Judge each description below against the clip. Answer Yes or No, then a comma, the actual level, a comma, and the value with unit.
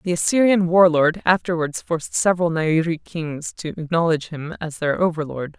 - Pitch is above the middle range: No, medium, 165 Hz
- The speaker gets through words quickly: No, average, 160 wpm